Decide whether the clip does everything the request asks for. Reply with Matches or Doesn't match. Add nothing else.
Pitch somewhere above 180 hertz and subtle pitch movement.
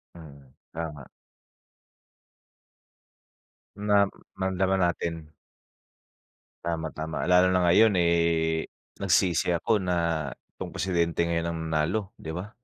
Doesn't match